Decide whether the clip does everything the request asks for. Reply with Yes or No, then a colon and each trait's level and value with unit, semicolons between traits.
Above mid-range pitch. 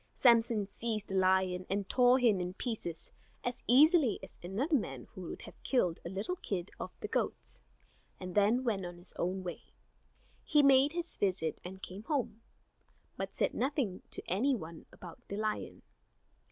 Yes: high, 205 Hz